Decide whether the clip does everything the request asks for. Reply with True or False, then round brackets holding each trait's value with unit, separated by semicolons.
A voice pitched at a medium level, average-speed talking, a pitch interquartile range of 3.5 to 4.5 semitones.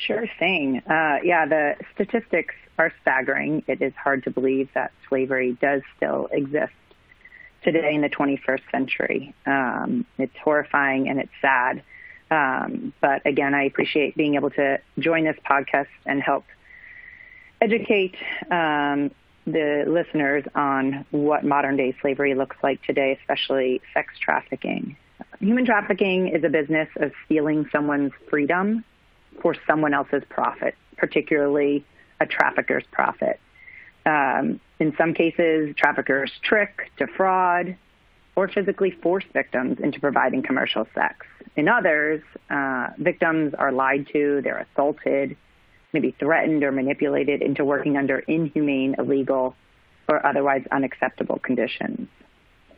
False (145 Hz; 125 wpm; 3.8 semitones)